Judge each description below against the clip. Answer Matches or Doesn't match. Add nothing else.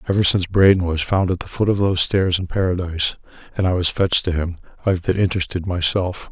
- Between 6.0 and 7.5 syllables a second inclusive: Matches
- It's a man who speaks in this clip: Matches